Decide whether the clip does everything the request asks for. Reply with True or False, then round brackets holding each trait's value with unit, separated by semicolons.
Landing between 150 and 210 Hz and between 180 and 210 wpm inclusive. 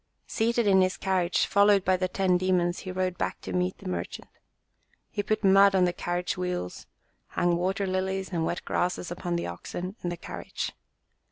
True (185 Hz; 185 wpm)